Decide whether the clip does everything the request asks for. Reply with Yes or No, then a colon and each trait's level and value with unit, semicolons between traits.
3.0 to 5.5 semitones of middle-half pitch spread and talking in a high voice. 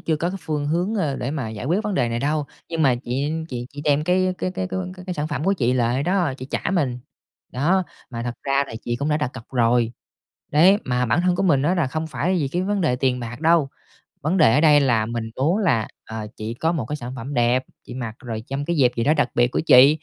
No: average, 5.2 semitones; medium, 140 Hz